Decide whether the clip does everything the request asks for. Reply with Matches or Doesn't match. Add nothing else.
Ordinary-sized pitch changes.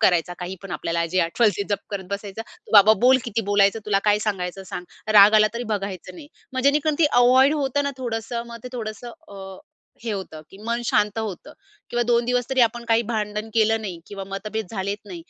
Matches